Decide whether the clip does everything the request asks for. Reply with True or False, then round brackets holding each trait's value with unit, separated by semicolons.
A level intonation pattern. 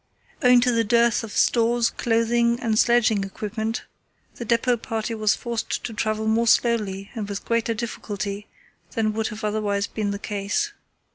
True (1.9 semitones)